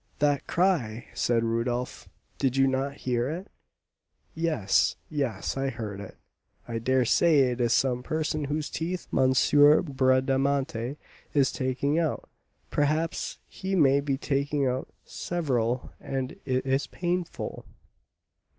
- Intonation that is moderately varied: Yes, average, 3.1 semitones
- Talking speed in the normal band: No, slow, 125 wpm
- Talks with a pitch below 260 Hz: Yes, low, 135 Hz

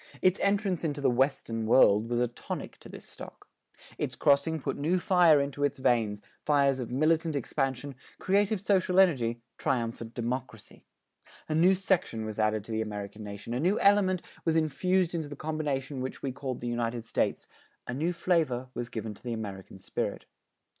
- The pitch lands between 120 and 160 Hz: Yes, low, 135 Hz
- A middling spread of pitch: No, wide, 6.0 semitones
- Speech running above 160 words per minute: Yes, average, 175 wpm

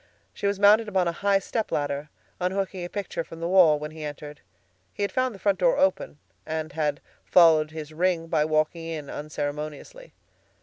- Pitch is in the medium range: Yes, medium, 165 Hz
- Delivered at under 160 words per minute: No, average, 180 wpm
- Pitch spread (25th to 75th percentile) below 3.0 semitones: No, average, 4.0 semitones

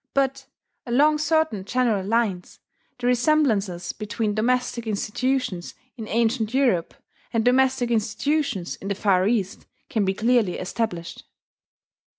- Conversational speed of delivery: No, slow, 120 wpm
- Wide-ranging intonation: No, average, 4.1 semitones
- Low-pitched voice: No, high, 230 Hz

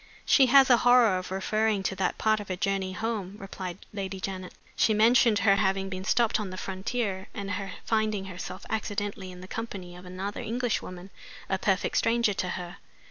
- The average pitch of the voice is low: No, high, 195 Hz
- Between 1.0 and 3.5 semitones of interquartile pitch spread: Yes, average, 2.7 semitones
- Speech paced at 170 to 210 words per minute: Yes, average, 190 wpm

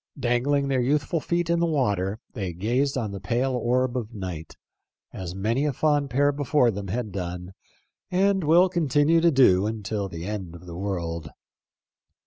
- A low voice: Yes, low, 120 Hz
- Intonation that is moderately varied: No, wide, 6.9 semitones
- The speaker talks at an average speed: Yes, average, 170 wpm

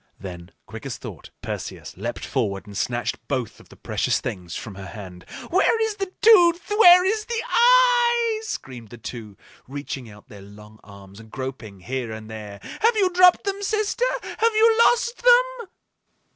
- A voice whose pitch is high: No, low, 135 Hz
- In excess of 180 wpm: No, average, 170 wpm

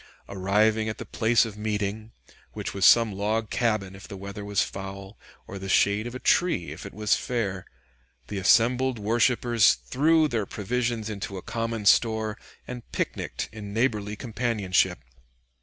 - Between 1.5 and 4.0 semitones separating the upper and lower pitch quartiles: Yes, average, 2.7 semitones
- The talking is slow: No, average, 155 wpm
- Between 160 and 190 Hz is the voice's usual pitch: No, low, 110 Hz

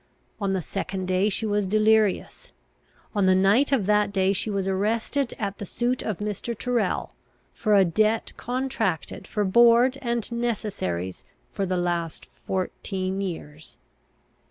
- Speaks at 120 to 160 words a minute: Yes, average, 145 wpm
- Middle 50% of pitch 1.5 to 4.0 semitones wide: Yes, average, 3.3 semitones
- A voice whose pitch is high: Yes, high, 205 Hz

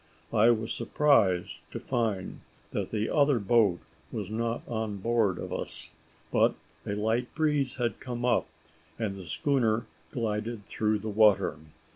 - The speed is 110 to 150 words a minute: Yes, average, 145 wpm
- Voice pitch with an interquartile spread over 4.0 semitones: No, narrow, 2.5 semitones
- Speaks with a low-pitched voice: Yes, low, 110 Hz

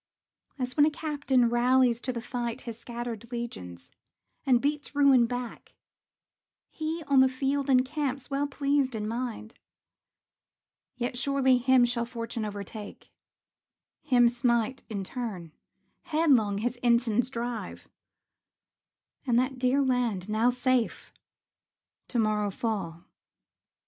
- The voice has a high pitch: Yes, high, 245 Hz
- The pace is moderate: No, slow, 120 wpm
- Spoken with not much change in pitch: Yes, narrow, 2.3 semitones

